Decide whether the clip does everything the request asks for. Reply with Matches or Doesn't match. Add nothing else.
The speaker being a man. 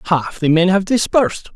Matches